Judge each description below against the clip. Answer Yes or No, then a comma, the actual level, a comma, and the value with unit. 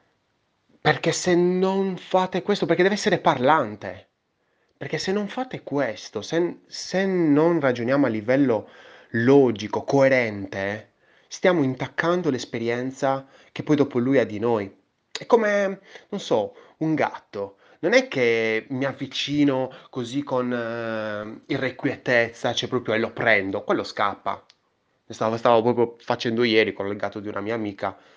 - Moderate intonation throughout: No, wide, 7.0 semitones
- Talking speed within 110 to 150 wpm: Yes, average, 140 wpm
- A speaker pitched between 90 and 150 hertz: Yes, low, 135 Hz